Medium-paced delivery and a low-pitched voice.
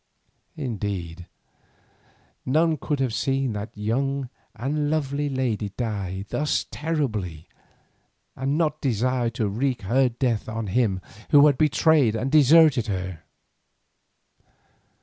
No: slow, 110 wpm; low, 130 Hz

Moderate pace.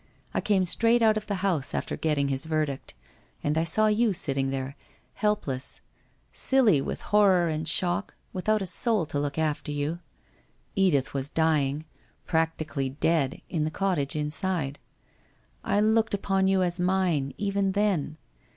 Yes: average, 160 wpm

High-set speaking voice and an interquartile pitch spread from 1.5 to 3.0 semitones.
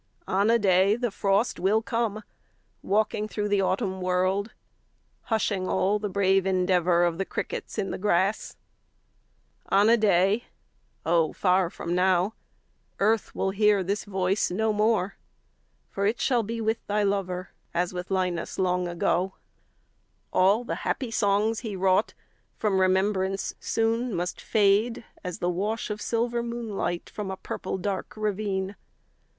Yes: high, 195 Hz; narrow, 2.5 semitones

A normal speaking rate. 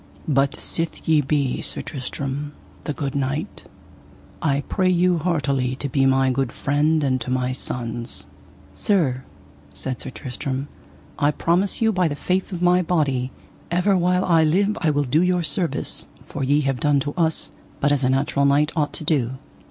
Yes: average, 175 wpm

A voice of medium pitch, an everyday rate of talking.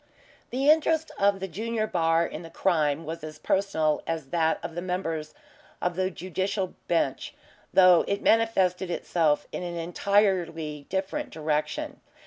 Yes: medium, 175 Hz; average, 145 wpm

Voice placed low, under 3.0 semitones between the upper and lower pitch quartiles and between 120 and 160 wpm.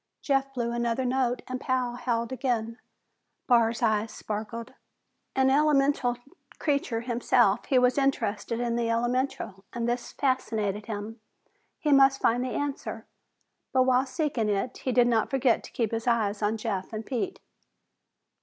No: high, 240 Hz; narrow, 2.5 semitones; average, 150 wpm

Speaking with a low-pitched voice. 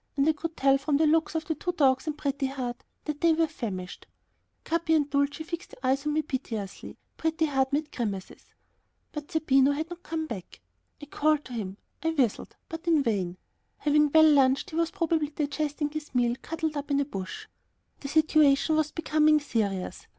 No: very high, 295 Hz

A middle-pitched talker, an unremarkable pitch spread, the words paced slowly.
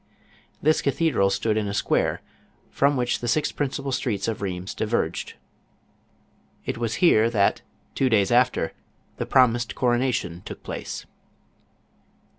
No: low, 120 Hz; average, 4.1 semitones; slow, 130 wpm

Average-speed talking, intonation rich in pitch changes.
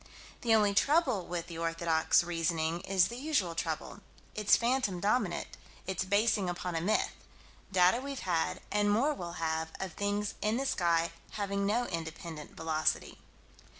No: average, 150 wpm; average, 4.2 semitones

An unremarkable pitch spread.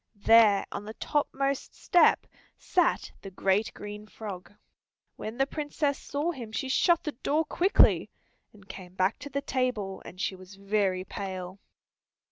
No: wide, 6.3 semitones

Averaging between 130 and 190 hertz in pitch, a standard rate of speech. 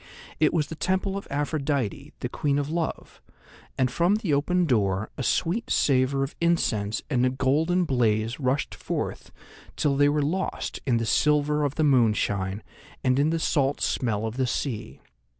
Yes: medium, 140 Hz; average, 170 wpm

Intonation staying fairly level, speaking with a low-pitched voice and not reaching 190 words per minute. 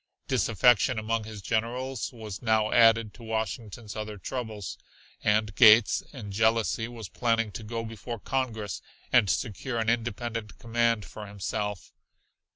Yes: narrow, 1.7 semitones; low, 110 Hz; slow, 135 wpm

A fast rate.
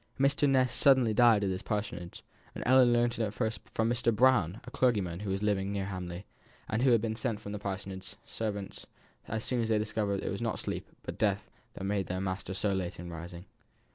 Yes: fast, 225 wpm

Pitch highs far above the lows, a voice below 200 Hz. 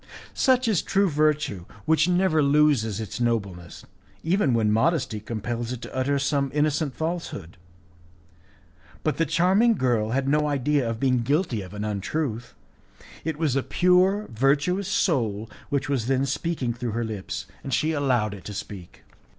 Yes: wide, 5.8 semitones; low, 135 Hz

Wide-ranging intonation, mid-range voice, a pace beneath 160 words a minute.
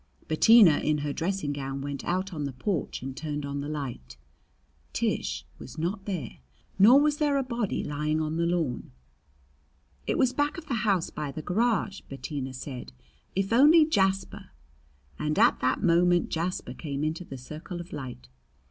No: wide, 5.8 semitones; medium, 160 Hz; average, 175 wpm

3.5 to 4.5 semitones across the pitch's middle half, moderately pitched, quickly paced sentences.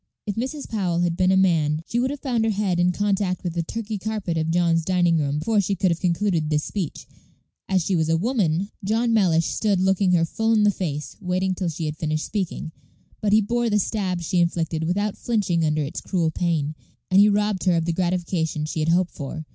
Yes: average, 3.9 semitones; medium, 180 Hz; fast, 225 wpm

